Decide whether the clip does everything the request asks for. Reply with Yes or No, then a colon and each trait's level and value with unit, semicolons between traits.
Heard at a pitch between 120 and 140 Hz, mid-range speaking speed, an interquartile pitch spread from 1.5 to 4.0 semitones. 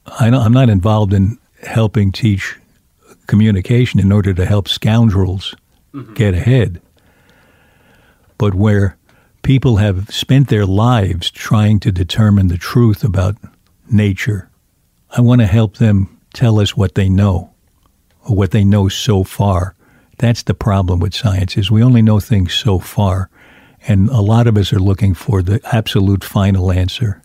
No: low, 105 Hz; average, 155 wpm; average, 2.9 semitones